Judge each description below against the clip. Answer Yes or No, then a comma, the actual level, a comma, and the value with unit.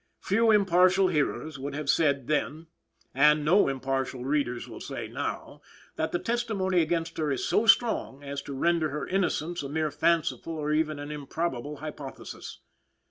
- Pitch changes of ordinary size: Yes, average, 3.6 semitones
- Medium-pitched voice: Yes, medium, 155 Hz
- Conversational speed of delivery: Yes, average, 160 wpm